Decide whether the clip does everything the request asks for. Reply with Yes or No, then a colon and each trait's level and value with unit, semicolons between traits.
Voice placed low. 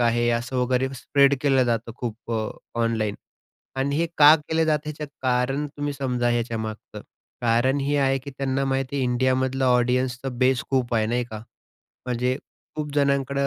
Yes: low, 130 Hz